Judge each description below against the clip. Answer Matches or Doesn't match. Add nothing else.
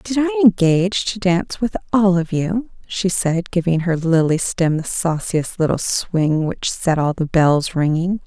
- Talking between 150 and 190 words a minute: Matches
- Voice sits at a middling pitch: Matches